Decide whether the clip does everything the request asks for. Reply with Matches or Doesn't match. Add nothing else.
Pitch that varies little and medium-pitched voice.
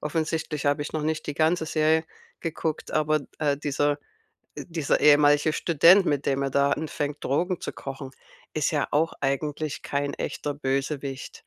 Matches